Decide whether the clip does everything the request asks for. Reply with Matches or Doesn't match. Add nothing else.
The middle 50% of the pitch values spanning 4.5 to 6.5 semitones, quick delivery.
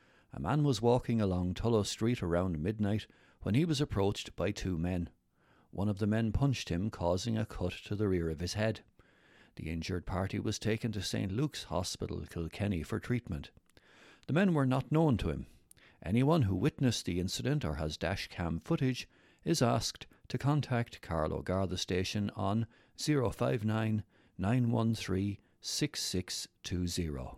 Doesn't match